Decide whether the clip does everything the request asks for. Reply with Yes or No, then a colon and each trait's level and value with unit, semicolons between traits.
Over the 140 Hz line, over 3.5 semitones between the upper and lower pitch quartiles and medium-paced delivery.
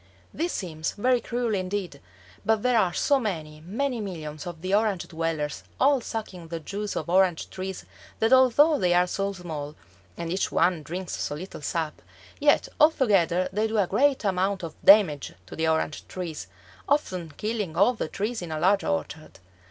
Yes: medium, 185 Hz; average, 5.0 semitones; average, 175 wpm